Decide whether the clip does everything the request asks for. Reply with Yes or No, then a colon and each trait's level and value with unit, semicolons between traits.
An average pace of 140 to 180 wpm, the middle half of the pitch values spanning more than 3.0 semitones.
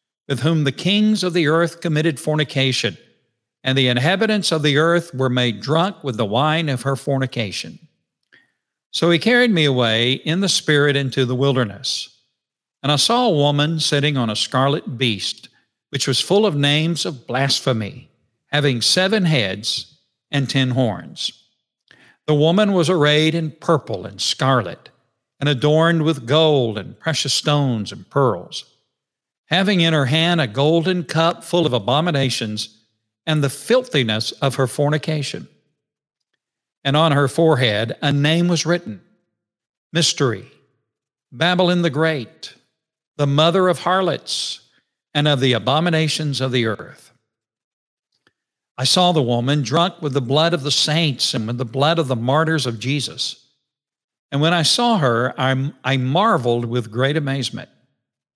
Yes: average, 150 wpm; average, 4.0 semitones